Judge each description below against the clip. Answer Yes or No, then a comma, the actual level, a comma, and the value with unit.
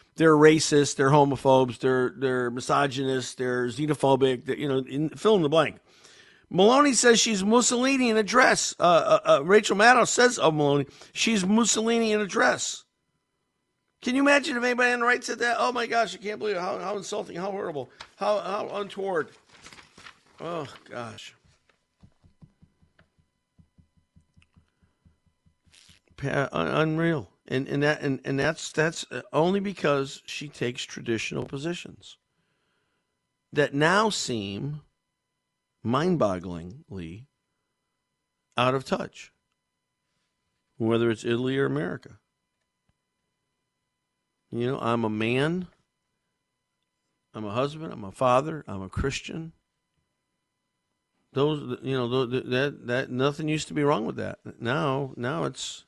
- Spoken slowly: Yes, slow, 130 wpm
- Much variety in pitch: Yes, wide, 8.3 semitones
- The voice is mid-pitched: Yes, medium, 145 Hz